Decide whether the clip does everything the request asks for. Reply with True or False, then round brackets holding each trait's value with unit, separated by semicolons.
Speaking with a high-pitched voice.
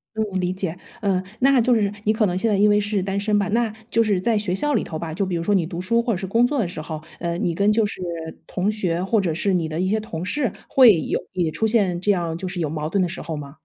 True (195 Hz)